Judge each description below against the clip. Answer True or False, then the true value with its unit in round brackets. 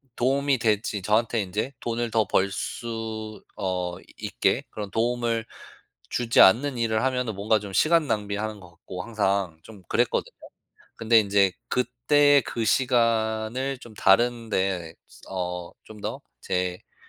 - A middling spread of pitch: True (3.2 semitones)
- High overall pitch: False (110 Hz)